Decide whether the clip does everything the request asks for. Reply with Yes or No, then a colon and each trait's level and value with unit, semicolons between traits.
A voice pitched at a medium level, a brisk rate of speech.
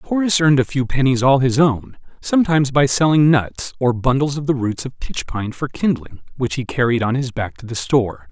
No: low, 130 Hz; fast, 225 wpm